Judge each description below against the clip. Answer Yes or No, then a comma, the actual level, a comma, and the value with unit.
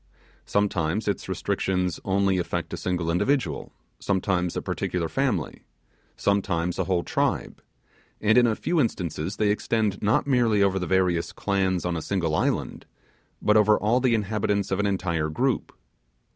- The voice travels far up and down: No, average, 3.2 semitones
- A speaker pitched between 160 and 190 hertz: No, very low, 95 Hz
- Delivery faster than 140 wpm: Yes, average, 155 wpm